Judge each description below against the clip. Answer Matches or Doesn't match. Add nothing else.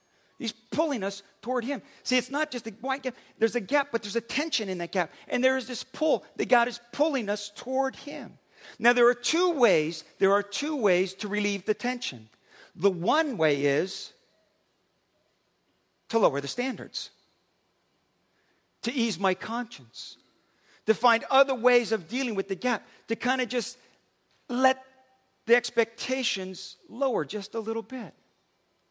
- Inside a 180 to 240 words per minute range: Doesn't match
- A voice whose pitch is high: Matches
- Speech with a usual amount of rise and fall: Matches